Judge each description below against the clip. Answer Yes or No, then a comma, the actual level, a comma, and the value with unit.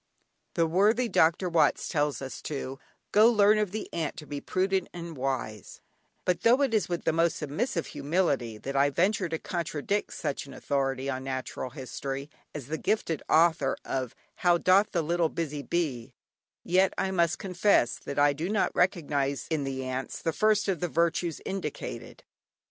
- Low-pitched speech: No, medium, 165 Hz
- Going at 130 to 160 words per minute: No, average, 175 wpm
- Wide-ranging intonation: No, average, 4.9 semitones